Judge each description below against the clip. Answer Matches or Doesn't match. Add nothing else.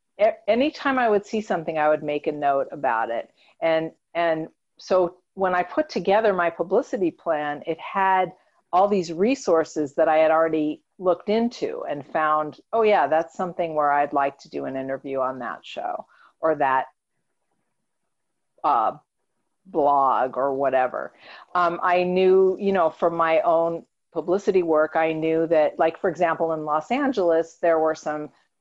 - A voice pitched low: Doesn't match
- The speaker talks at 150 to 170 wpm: Matches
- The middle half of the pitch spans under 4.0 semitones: Matches